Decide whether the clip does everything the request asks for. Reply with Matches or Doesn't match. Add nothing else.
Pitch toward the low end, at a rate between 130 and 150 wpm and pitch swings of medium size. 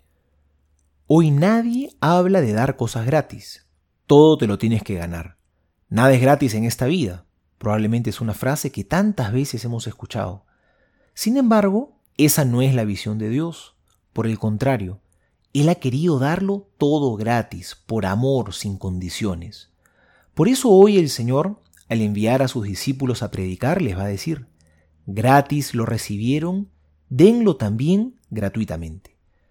Doesn't match